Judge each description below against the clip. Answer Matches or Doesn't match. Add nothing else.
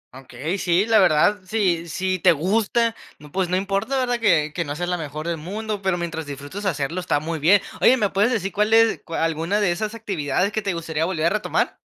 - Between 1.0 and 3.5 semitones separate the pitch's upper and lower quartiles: Doesn't match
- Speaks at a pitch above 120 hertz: Matches